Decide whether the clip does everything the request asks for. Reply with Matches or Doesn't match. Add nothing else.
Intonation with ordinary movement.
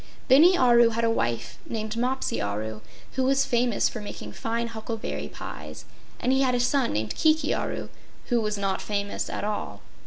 Matches